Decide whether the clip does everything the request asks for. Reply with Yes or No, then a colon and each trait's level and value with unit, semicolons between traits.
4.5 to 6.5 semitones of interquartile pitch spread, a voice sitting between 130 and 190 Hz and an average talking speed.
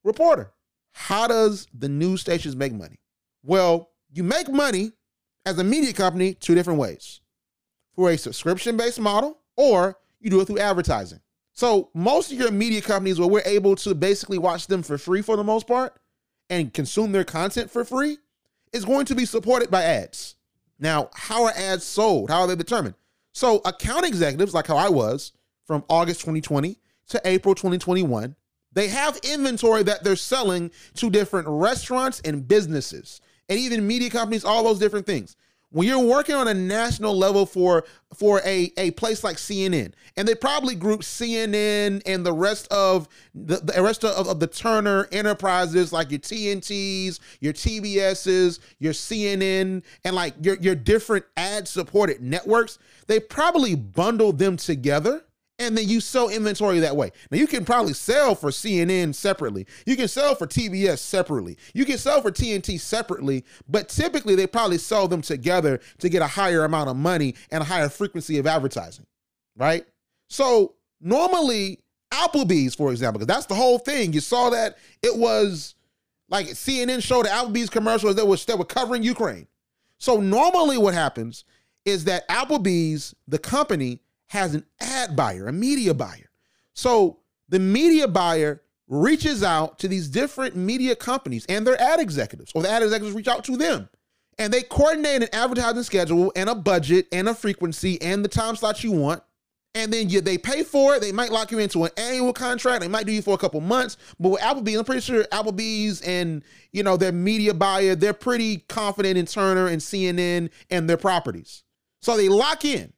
No: average, 4.8 semitones; high, 200 Hz; average, 180 wpm